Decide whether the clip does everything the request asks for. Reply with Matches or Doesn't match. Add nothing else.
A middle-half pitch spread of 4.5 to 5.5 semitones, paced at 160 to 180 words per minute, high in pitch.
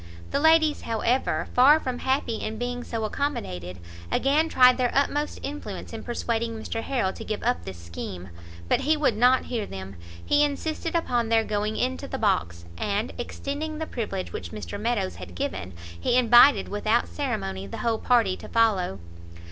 Matches